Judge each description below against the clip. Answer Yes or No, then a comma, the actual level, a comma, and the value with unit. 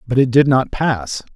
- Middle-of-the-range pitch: No, low, 125 Hz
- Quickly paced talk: Yes, fast, 220 wpm